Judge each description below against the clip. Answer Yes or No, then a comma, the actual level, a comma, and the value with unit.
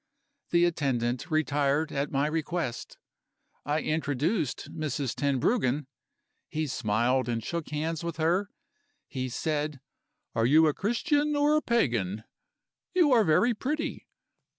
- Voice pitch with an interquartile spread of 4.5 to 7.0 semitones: Yes, average, 4.8 semitones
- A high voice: No, medium, 155 Hz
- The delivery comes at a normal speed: No, slow, 125 wpm